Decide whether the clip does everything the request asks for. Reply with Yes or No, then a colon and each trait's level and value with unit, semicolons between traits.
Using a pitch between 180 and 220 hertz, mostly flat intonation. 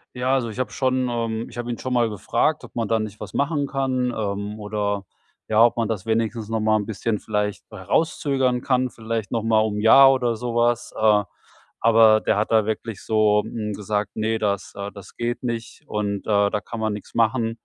No: low, 110 Hz; narrow, 2.3 semitones